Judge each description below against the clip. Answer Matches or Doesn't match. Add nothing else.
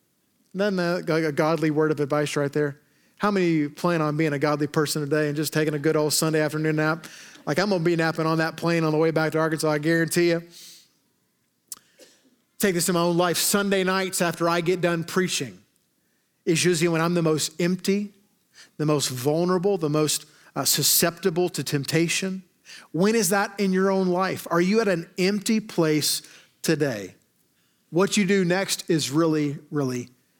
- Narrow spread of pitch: Doesn't match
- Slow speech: Doesn't match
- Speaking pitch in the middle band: Matches